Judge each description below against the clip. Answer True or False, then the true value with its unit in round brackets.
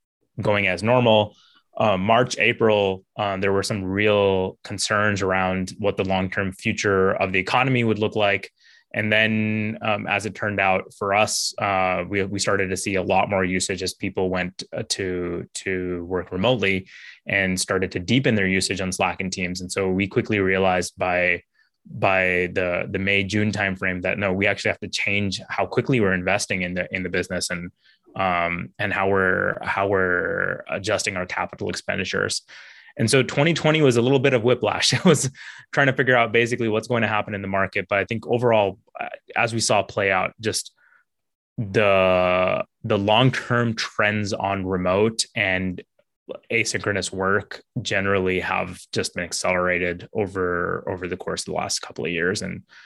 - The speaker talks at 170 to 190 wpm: True (175 wpm)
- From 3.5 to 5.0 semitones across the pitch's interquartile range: False (2.6 semitones)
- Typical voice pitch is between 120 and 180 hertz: False (100 Hz)